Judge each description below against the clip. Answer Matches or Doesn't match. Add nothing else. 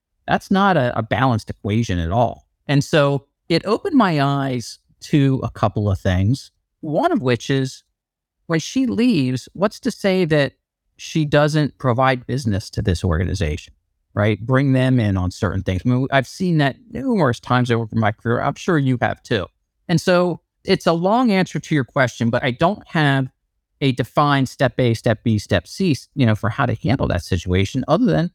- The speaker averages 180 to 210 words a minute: Matches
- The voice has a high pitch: Doesn't match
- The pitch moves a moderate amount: Doesn't match